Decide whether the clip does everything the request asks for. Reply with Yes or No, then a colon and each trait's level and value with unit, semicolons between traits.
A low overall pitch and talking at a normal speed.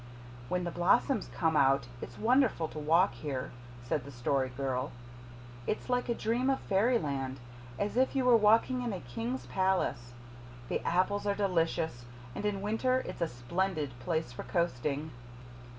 No: medium, 170 Hz; average, 160 wpm